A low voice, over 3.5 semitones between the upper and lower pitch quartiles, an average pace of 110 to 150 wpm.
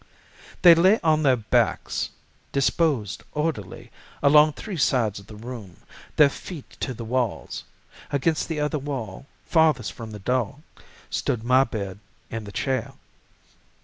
Yes: low, 130 Hz; average, 5.3 semitones; slow, 135 wpm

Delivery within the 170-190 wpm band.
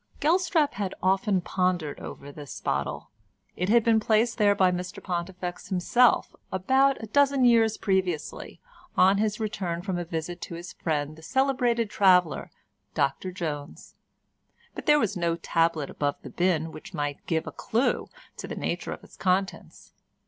No: average, 155 wpm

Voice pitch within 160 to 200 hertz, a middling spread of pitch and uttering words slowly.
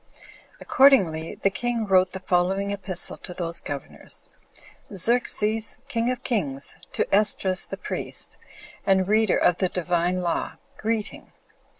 Yes: high, 190 Hz; average, 3.6 semitones; slow, 125 wpm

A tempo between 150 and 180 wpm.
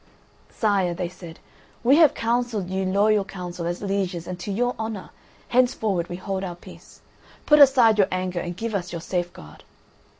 Yes: average, 175 wpm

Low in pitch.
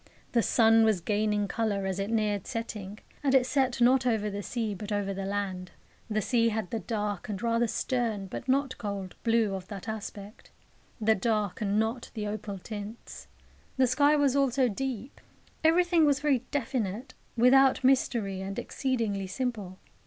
No: high, 220 Hz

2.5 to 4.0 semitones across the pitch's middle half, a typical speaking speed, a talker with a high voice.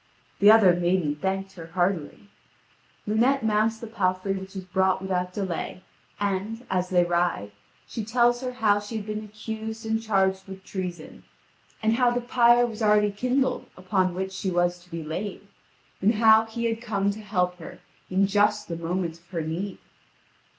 Yes: average, 3.3 semitones; average, 175 wpm; high, 195 Hz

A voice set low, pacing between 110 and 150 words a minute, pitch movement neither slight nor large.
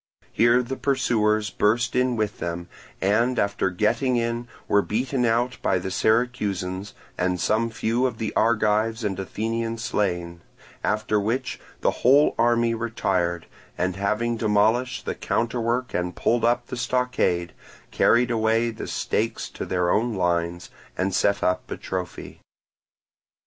Yes: low, 110 Hz; average, 140 wpm; average, 3.5 semitones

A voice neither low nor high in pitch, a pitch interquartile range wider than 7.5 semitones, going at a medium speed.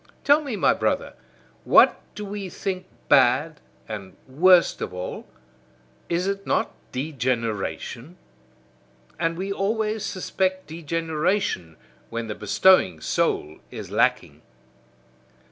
No: medium, 165 Hz; wide, 8.6 semitones; slow, 110 wpm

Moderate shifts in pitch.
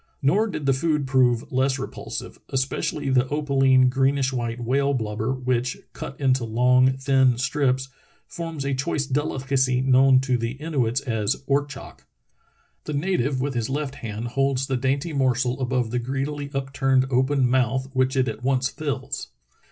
No: narrow, 1.6 semitones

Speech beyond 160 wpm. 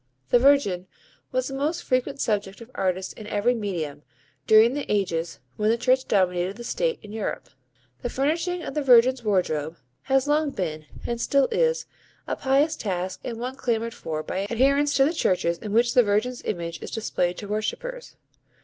Yes: average, 180 wpm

